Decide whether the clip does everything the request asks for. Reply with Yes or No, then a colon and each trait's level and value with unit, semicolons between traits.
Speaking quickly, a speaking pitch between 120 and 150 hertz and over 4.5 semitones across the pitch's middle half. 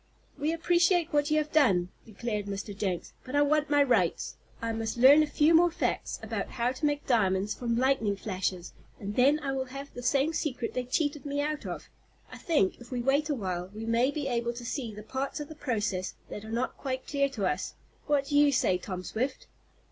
No: fast, 220 wpm; very high, 260 Hz; average, 5.0 semitones